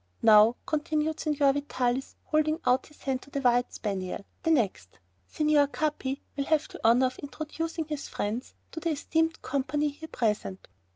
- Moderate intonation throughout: Yes, average, 3.9 semitones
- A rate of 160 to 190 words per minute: Yes, average, 165 wpm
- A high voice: Yes, very high, 280 Hz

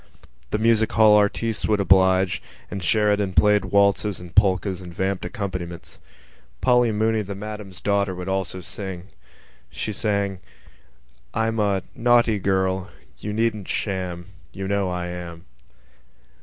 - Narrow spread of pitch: Yes, narrow, 2.2 semitones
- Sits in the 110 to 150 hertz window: No, low, 100 Hz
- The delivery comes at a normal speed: No, slow, 130 wpm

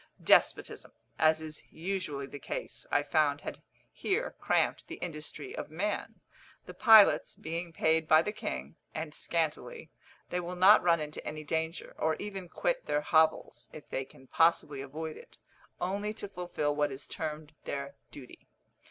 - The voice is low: No, medium, 160 Hz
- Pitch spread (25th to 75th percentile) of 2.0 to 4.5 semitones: Yes, average, 3.5 semitones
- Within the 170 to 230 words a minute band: No, average, 160 wpm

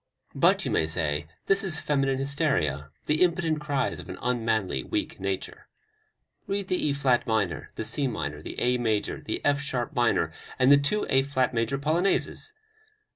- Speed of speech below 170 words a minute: No, average, 175 wpm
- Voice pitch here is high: No, low, 135 Hz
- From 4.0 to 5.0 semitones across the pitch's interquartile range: No, wide, 5.4 semitones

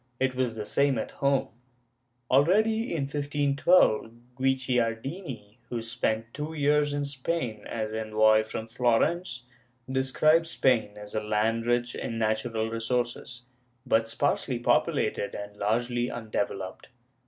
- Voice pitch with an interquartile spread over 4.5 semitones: No, average, 4.0 semitones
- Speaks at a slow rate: Yes, slow, 120 wpm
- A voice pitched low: Yes, low, 120 Hz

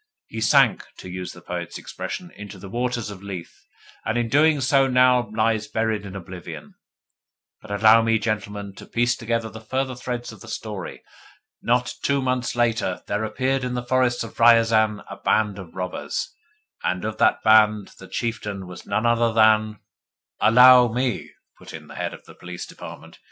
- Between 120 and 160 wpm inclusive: No, average, 180 wpm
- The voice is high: No, low, 110 Hz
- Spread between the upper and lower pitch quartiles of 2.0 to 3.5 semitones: Yes, average, 3.0 semitones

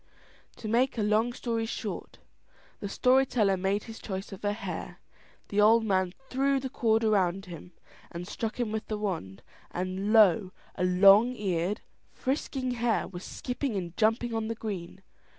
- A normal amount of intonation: Yes, average, 3.4 semitones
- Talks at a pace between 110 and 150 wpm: No, average, 165 wpm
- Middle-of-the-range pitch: No, high, 215 Hz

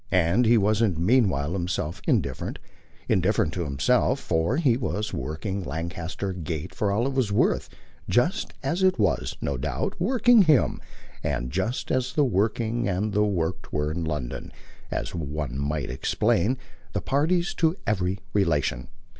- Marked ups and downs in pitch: Yes, wide, 7.2 semitones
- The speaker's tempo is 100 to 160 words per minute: Yes, average, 150 wpm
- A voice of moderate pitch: No, very low, 95 Hz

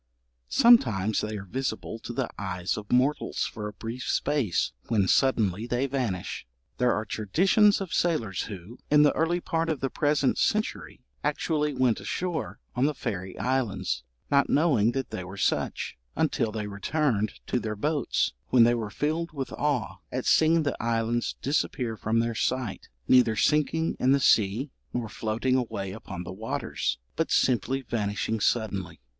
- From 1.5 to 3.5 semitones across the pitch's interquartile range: No, average, 5.2 semitones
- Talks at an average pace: Yes, average, 160 wpm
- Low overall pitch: Yes, low, 120 Hz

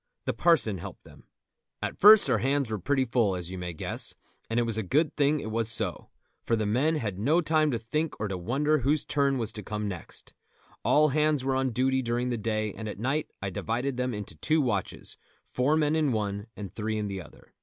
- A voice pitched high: No, low, 120 Hz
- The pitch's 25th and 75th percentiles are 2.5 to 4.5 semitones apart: No, average, 5.3 semitones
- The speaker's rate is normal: No, fast, 230 wpm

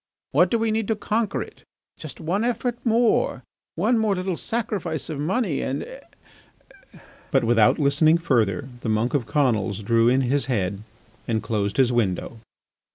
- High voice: No, medium, 145 Hz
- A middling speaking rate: Yes, average, 160 wpm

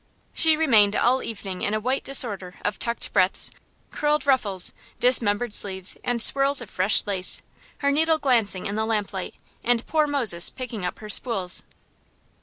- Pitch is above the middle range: Yes, high, 225 Hz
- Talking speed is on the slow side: No, average, 160 wpm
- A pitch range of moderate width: Yes, average, 4.9 semitones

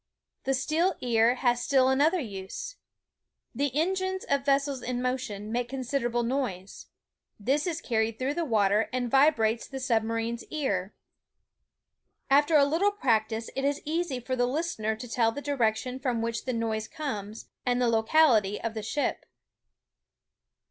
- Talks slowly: No, average, 160 wpm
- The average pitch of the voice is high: Yes, very high, 250 Hz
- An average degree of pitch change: Yes, average, 4.0 semitones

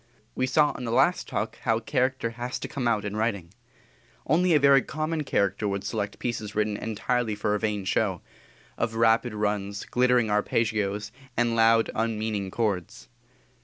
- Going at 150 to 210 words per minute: Yes, average, 165 wpm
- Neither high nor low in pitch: No, low, 115 Hz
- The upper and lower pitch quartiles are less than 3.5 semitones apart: Yes, average, 2.9 semitones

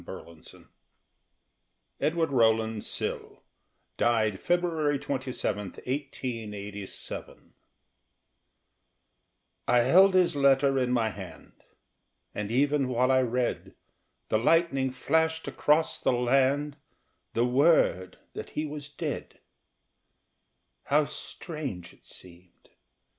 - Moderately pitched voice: No, low, 130 Hz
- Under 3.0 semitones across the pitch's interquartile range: No, average, 4.8 semitones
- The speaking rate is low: Yes, slow, 95 wpm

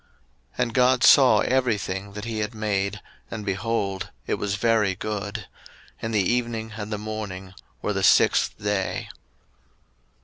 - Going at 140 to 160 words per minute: Yes, average, 150 wpm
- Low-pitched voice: Yes, low, 105 Hz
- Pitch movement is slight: Yes, narrow, 2.3 semitones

